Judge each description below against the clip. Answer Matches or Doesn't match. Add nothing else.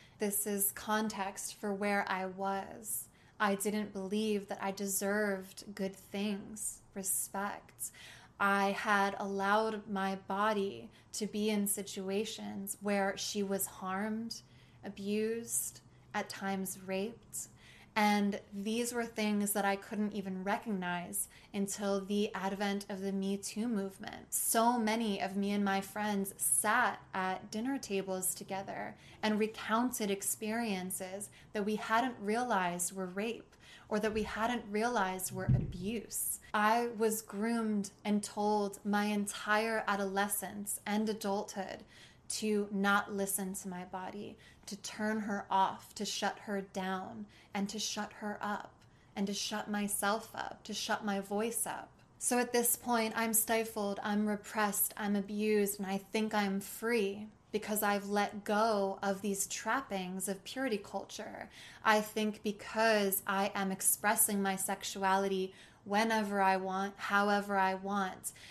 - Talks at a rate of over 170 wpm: Doesn't match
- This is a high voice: Matches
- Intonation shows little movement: Matches